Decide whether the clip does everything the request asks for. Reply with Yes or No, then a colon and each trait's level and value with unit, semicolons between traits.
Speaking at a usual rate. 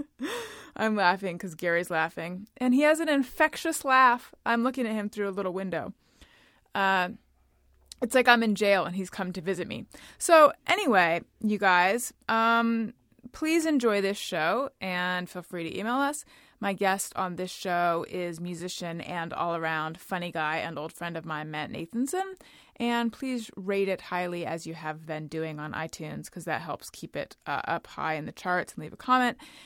Yes: average, 185 wpm